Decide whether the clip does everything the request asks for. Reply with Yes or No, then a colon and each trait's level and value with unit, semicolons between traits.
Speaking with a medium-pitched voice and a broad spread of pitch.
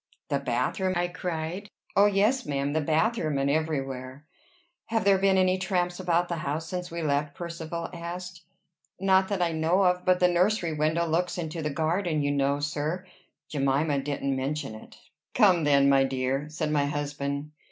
No: medium, 160 Hz; average, 3.9 semitones